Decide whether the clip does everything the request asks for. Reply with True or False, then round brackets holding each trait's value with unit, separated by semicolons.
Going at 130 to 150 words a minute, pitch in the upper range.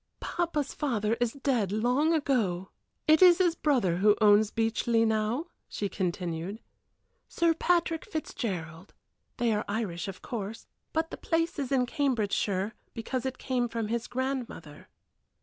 True (140 wpm; 230 Hz)